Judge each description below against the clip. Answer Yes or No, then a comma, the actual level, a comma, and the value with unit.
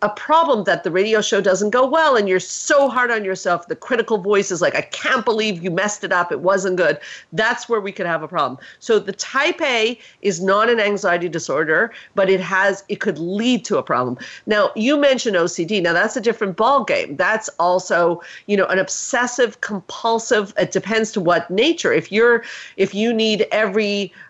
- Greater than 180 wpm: Yes, fast, 205 wpm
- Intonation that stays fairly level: No, average, 3.7 semitones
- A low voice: No, high, 205 Hz